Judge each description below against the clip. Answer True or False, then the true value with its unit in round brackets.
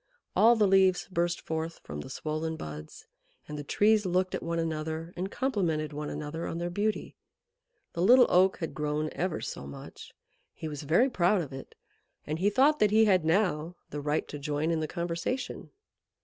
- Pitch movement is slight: False (3.9 semitones)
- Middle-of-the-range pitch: True (170 Hz)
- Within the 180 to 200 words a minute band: True (190 wpm)